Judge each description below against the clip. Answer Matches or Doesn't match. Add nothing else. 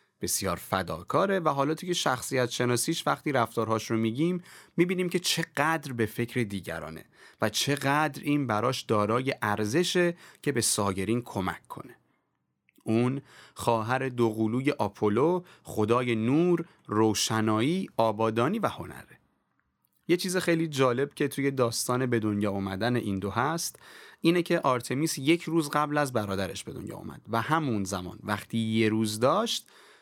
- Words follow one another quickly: Doesn't match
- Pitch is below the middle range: Matches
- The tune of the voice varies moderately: Doesn't match